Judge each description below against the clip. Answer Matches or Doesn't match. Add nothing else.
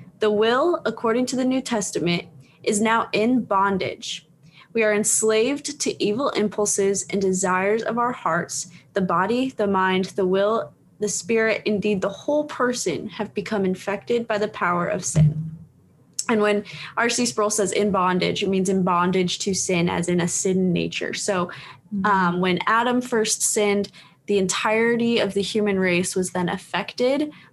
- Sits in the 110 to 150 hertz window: Doesn't match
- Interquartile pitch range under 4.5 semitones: Matches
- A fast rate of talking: Doesn't match